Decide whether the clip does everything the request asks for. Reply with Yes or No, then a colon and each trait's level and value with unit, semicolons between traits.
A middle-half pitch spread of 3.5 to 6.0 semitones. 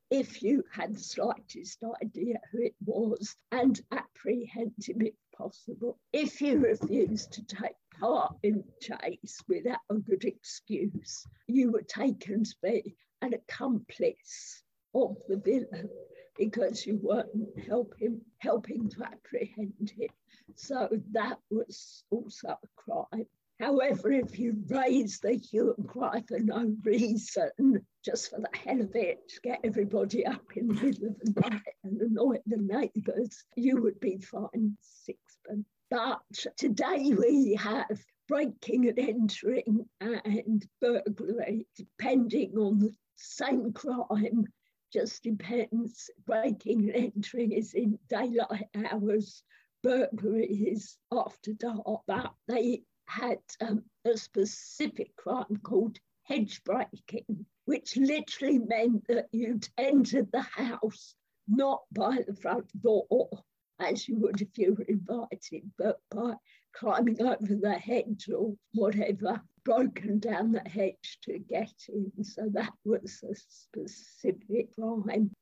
No: narrow, 2.4 semitones